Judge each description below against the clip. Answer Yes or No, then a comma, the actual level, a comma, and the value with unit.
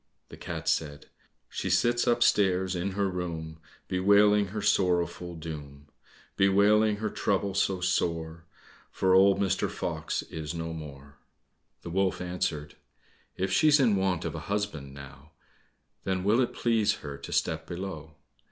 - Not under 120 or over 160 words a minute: Yes, average, 145 wpm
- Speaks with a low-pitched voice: Yes, very low, 90 Hz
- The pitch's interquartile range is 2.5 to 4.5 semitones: Yes, average, 4.0 semitones